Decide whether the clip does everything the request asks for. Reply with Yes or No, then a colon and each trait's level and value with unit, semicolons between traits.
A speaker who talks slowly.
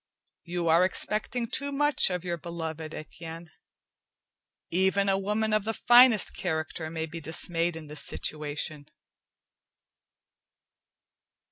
Yes: slow, 115 wpm